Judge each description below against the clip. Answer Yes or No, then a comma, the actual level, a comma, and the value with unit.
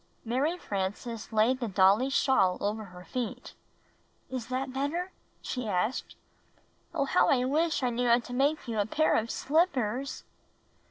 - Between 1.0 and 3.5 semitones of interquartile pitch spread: No, average, 4.0 semitones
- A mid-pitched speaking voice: No, high, 245 Hz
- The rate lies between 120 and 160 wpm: Yes, average, 155 wpm